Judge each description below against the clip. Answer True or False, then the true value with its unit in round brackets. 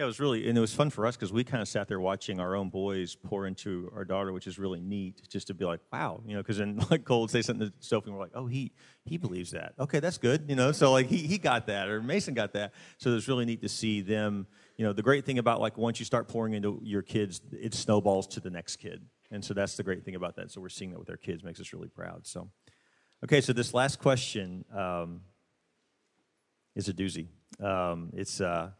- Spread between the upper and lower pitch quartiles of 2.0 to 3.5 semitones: False (3.9 semitones)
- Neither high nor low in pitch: False (105 Hz)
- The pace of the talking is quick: True (265 wpm)